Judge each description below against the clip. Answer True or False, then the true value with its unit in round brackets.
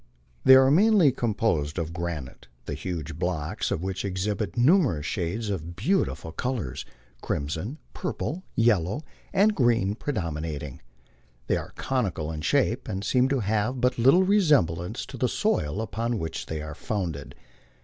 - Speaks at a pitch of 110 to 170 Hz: False (100 Hz)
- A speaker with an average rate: True (150 wpm)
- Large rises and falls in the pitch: True (7.8 semitones)